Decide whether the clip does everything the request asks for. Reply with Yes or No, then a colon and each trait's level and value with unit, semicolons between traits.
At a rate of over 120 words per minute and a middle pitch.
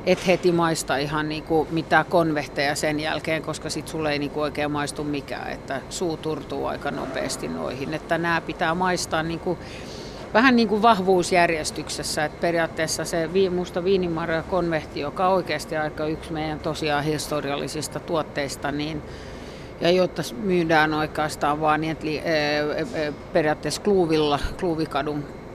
Yes: average, 130 wpm; medium, 155 Hz